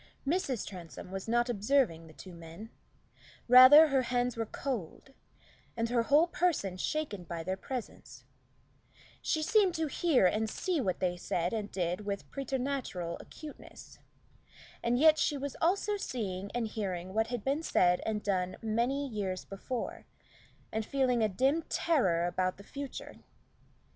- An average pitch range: No, wide, 6.8 semitones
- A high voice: Yes, high, 230 Hz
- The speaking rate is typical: Yes, average, 150 wpm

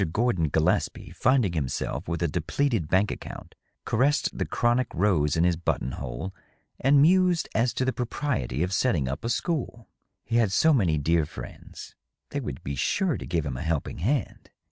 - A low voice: Yes, very low, 95 Hz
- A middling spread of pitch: No, wide, 8.5 semitones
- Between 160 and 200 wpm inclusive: Yes, average, 185 wpm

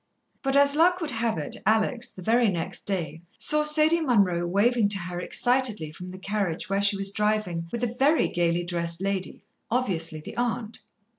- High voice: Yes, high, 205 Hz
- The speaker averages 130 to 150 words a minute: No, average, 180 wpm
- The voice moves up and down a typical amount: No, wide, 5.7 semitones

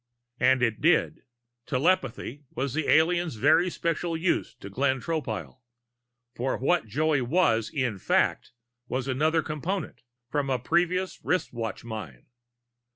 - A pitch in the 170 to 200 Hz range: No, medium, 140 Hz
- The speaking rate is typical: No, slow, 125 wpm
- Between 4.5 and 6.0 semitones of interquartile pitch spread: Yes, average, 5.1 semitones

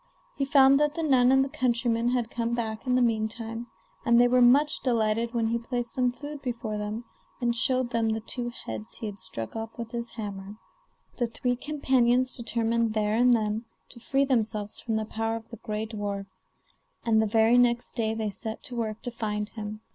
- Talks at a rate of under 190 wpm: No, fast, 205 wpm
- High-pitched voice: Yes, high, 230 Hz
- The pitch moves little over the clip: Yes, narrow, 2.1 semitones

